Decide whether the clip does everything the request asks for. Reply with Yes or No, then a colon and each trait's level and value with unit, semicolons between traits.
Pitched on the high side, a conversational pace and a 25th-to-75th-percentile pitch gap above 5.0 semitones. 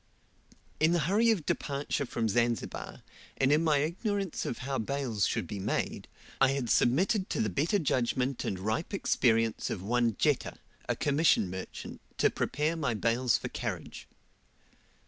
No: low, 135 Hz; average, 155 wpm; wide, 5.6 semitones